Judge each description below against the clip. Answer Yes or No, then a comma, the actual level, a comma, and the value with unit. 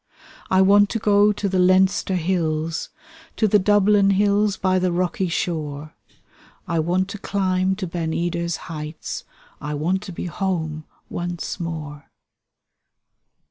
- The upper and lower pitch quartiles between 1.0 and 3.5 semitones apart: Yes, average, 2.9 semitones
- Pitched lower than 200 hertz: Yes, medium, 185 Hz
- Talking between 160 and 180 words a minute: No, average, 140 wpm